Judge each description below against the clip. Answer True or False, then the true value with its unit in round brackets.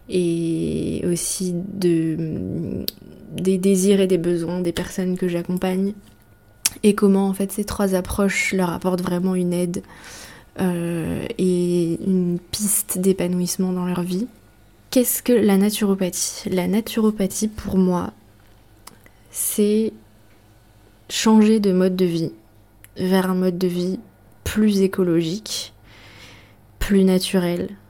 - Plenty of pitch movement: False (3.0 semitones)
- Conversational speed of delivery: False (120 wpm)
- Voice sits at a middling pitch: True (180 Hz)